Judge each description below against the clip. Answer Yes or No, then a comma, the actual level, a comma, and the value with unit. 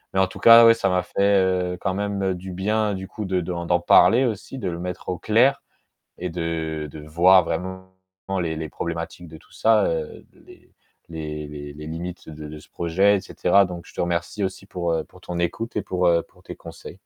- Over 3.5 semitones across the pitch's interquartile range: No, average, 2.8 semitones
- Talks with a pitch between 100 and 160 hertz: No, very low, 90 Hz